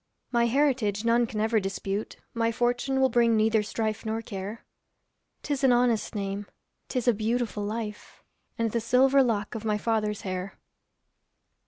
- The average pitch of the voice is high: Yes, high, 225 Hz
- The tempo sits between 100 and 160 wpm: Yes, average, 155 wpm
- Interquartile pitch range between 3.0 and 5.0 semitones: No, narrow, 2.4 semitones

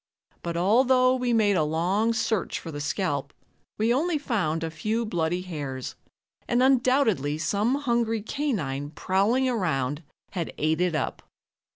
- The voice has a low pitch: No, high, 195 Hz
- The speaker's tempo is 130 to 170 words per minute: Yes, average, 145 wpm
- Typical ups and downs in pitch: No, wide, 7.2 semitones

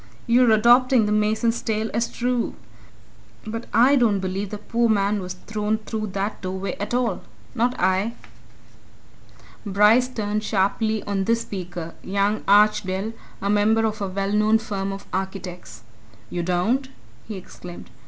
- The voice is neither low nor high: No, high, 210 Hz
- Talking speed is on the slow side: No, average, 145 wpm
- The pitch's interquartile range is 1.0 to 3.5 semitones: Yes, narrow, 2.6 semitones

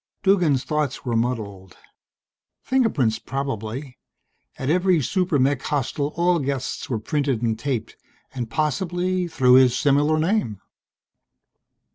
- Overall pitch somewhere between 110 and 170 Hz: Yes, medium, 140 Hz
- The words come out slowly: Yes, slow, 115 wpm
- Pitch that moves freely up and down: No, average, 5.0 semitones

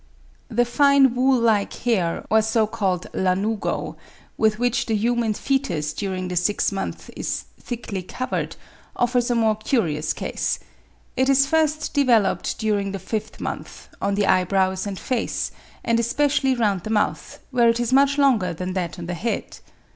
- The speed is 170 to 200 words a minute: No, average, 160 wpm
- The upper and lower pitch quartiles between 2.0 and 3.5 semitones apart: No, average, 4.3 semitones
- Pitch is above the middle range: Yes, high, 220 Hz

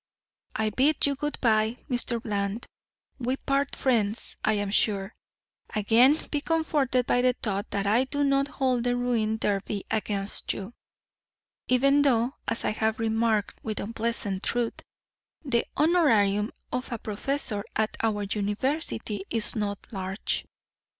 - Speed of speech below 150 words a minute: Yes, average, 140 wpm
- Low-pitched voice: No, high, 225 Hz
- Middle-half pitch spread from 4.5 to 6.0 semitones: No, average, 3.9 semitones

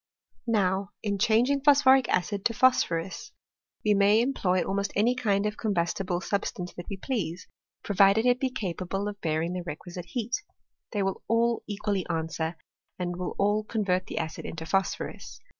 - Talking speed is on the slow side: No, average, 165 wpm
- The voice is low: No, high, 200 Hz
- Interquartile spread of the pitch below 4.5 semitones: Yes, average, 3.7 semitones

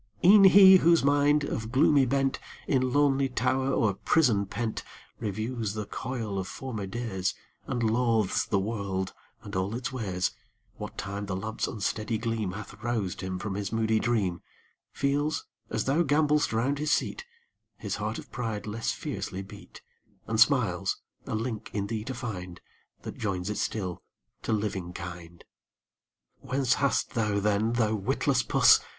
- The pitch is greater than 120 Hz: No, low, 110 Hz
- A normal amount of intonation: Yes, average, 4.6 semitones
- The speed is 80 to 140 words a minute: No, average, 155 wpm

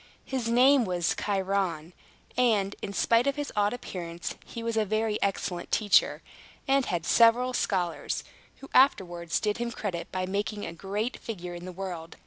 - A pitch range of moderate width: Yes, average, 4.6 semitones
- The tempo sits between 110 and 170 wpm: Yes, average, 165 wpm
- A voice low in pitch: No, high, 205 Hz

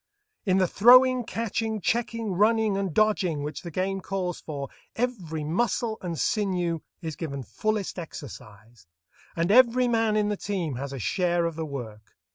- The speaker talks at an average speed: Yes, average, 160 wpm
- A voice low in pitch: No, medium, 185 Hz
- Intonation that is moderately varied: No, wide, 5.7 semitones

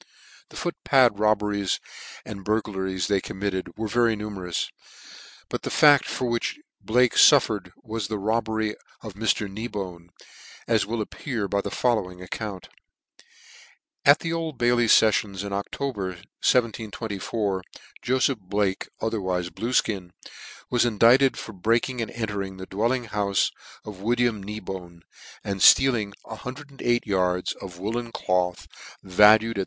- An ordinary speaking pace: No, slow, 130 wpm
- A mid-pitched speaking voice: No, low, 105 Hz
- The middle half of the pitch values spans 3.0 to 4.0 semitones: Yes, average, 3.5 semitones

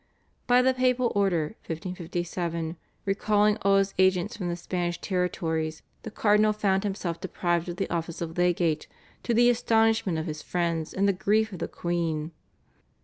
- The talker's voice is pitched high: No, medium, 180 Hz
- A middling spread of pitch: Yes, average, 3.7 semitones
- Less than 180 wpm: Yes, average, 160 wpm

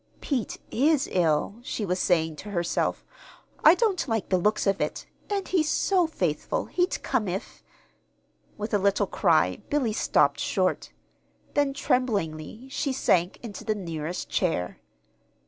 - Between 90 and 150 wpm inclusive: Yes, average, 145 wpm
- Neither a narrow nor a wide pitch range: No, wide, 7.5 semitones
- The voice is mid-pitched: No, high, 210 Hz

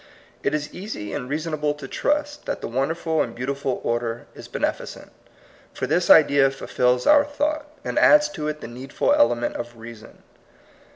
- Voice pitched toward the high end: No, medium, 140 Hz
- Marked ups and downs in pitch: Yes, wide, 5.8 semitones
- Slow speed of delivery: No, average, 170 wpm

